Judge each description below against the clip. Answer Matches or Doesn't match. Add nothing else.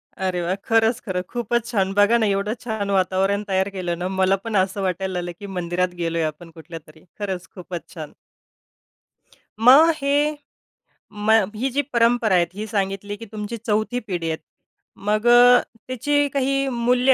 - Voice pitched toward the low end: Doesn't match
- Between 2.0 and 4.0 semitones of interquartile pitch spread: Doesn't match